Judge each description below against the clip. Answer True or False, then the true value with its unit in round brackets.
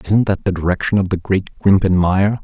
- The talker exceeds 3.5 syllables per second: True (5.2 syllables/s)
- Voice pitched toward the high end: False (95 Hz)